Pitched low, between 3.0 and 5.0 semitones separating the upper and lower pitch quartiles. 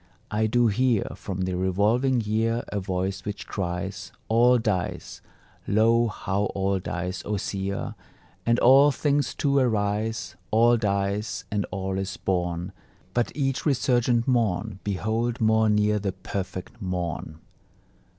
Yes: low, 105 Hz; average, 3.5 semitones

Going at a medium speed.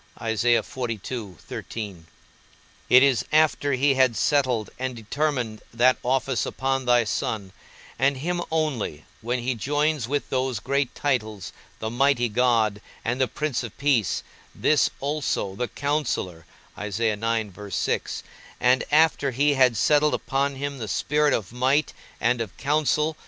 No: slow, 130 wpm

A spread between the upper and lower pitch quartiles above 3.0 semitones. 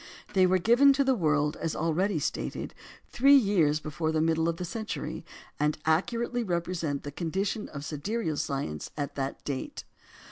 Yes: wide, 5.5 semitones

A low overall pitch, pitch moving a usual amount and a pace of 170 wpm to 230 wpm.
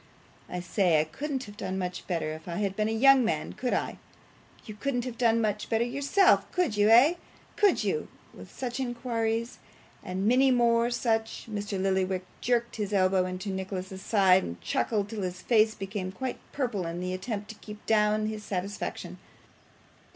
No: high, 210 Hz; average, 4.0 semitones; average, 180 wpm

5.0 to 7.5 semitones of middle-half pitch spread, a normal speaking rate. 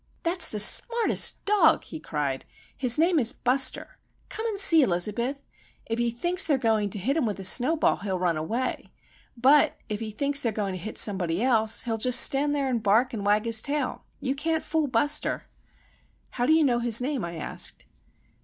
Yes: wide, 5.6 semitones; average, 190 wpm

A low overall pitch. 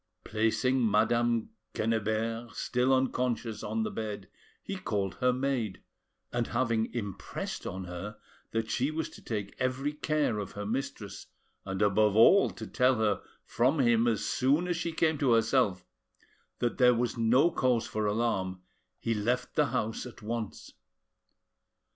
Yes: low, 115 Hz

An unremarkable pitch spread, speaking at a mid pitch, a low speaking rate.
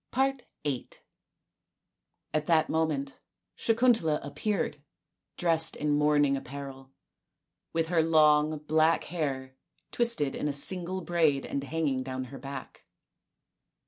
Yes: average, 3.0 semitones; medium, 150 Hz; slow, 110 wpm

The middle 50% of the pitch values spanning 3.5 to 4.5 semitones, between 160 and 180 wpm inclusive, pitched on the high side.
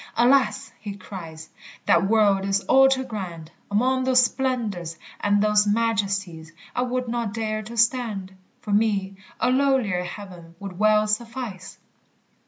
No: average, 3.8 semitones; average, 140 wpm; high, 210 Hz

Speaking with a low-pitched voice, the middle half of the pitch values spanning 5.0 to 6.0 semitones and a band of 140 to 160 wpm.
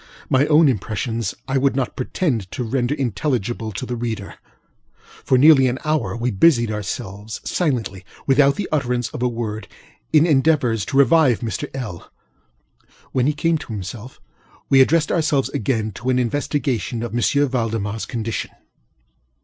No: low, 125 Hz; average, 3.9 semitones; average, 145 wpm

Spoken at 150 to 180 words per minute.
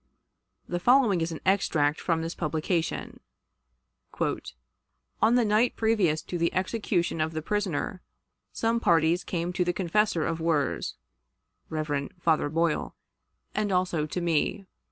No: slow, 135 wpm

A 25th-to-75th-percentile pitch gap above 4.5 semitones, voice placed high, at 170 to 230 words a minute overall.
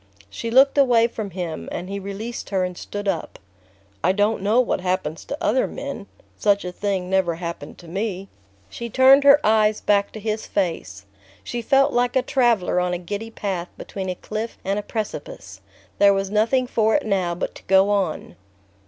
No: average, 3.9 semitones; high, 205 Hz; average, 190 wpm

